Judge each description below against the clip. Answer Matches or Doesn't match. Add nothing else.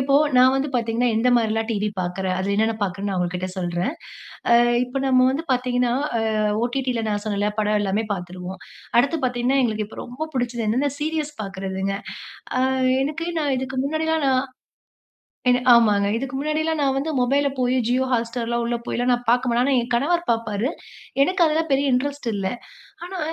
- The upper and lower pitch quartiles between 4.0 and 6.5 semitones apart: Matches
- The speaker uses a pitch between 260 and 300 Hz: Doesn't match